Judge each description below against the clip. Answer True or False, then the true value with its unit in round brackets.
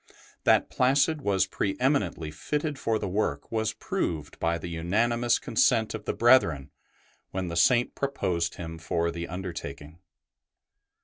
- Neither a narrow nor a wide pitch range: False (6.2 semitones)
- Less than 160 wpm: True (140 wpm)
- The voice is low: True (95 Hz)